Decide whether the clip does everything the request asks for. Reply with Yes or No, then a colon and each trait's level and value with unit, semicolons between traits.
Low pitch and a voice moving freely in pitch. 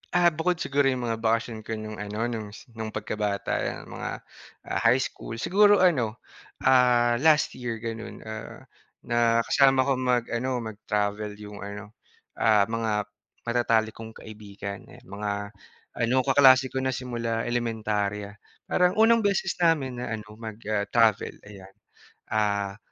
No: low, 115 Hz; average, 3.5 semitones